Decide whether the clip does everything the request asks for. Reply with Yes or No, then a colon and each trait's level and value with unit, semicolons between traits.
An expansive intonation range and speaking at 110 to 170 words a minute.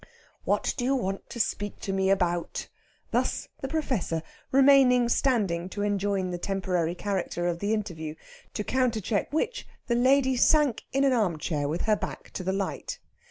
Yes: wide, 5.8 semitones; average, 165 wpm